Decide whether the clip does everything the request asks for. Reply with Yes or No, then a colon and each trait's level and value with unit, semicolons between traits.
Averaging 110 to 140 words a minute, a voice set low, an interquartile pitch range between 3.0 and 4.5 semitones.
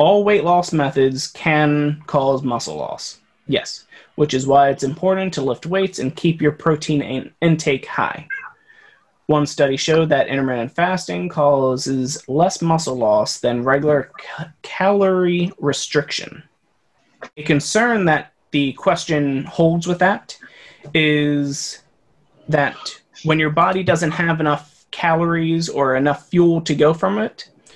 No: slow, 135 wpm; medium, 155 Hz; average, 3.6 semitones